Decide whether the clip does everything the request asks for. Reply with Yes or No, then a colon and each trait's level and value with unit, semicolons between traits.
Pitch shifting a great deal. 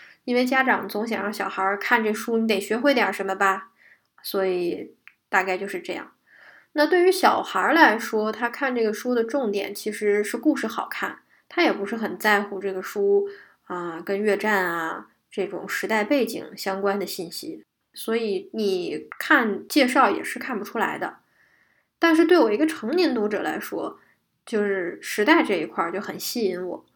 No: average, 4.3 semitones